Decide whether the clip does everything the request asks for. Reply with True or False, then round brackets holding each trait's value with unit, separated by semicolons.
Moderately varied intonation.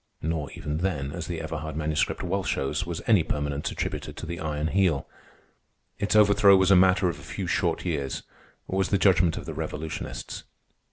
True (3.9 semitones)